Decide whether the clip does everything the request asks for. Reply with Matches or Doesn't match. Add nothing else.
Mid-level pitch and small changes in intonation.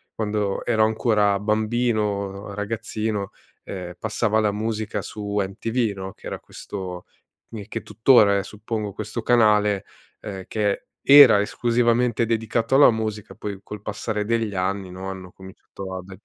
Doesn't match